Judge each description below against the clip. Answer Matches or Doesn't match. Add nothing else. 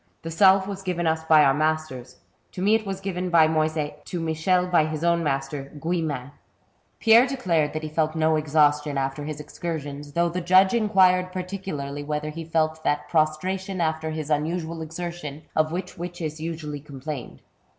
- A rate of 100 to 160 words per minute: Doesn't match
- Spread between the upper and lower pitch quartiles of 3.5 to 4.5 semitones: Doesn't match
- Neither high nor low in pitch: Matches